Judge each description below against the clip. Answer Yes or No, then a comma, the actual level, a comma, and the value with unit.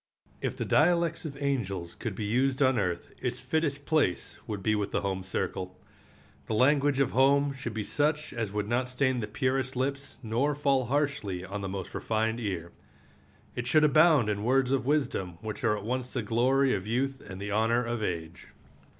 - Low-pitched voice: Yes, low, 125 Hz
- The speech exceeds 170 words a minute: Yes, average, 190 wpm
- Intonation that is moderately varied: Yes, average, 5.0 semitones